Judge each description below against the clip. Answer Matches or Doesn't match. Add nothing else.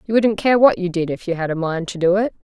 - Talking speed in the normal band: Doesn't match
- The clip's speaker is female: Matches